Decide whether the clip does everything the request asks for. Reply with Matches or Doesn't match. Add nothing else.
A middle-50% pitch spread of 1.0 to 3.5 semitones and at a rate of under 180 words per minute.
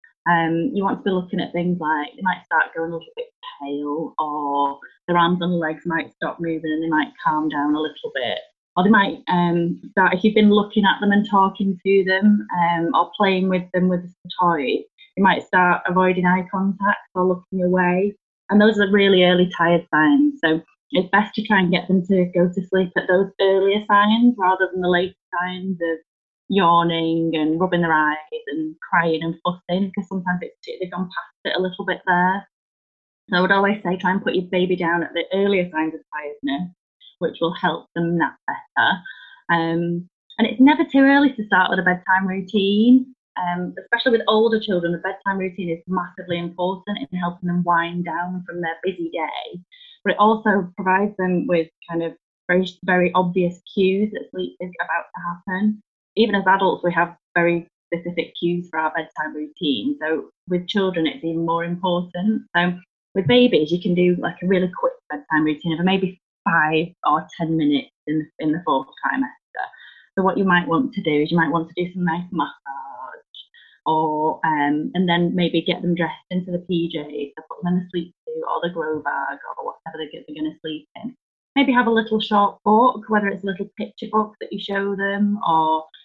Doesn't match